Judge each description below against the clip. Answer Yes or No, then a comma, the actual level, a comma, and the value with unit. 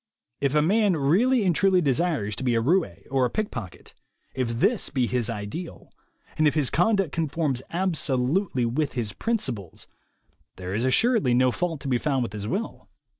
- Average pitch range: No, wide, 6.6 semitones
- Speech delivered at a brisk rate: No, average, 175 wpm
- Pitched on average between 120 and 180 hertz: Yes, medium, 140 Hz